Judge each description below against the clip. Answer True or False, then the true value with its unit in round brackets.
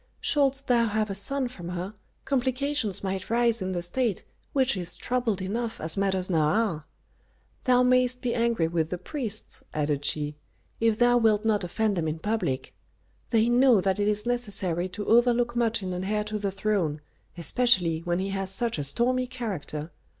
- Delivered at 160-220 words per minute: True (180 wpm)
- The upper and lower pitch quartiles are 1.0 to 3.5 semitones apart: False (5.0 semitones)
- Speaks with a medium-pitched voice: False (210 Hz)